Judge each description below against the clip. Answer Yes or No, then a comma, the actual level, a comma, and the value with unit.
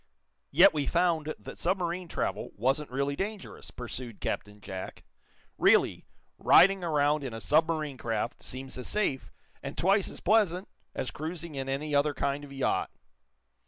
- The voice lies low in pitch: No, medium, 150 Hz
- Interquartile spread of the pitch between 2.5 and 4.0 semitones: No, average, 4.5 semitones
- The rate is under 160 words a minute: Yes, average, 150 wpm